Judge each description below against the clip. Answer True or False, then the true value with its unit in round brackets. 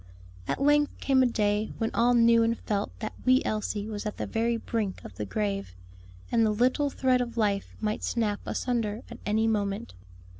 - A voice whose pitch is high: True (220 Hz)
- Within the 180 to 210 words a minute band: True (190 wpm)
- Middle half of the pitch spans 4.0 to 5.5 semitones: False (2.6 semitones)